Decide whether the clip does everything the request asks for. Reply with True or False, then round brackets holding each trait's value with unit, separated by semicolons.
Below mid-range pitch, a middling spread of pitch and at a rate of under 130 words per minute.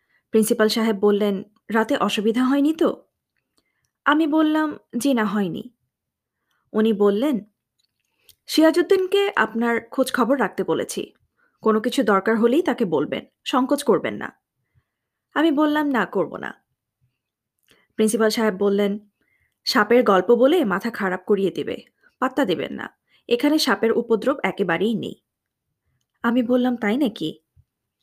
False (225 Hz; 4.7 semitones; 120 wpm)